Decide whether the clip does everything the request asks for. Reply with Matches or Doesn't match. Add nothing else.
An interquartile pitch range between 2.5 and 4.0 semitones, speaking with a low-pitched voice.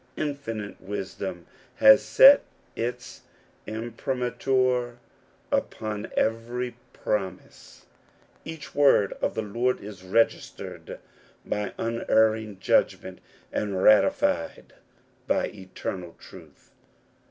Matches